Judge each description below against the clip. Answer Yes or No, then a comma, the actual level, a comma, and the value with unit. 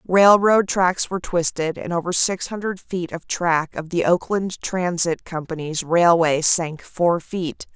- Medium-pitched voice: Yes, medium, 175 Hz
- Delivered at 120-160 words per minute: Yes, average, 155 wpm